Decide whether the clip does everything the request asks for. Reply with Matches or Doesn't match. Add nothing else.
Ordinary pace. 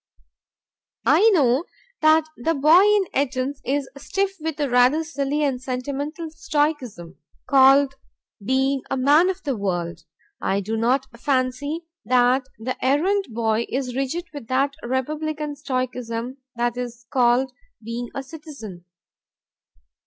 Doesn't match